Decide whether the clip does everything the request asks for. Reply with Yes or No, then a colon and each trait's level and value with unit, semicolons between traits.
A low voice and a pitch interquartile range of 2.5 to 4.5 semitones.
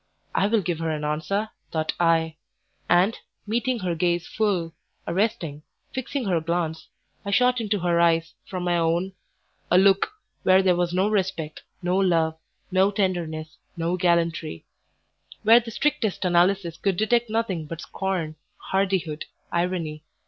No: medium, 180 Hz; average, 3.2 semitones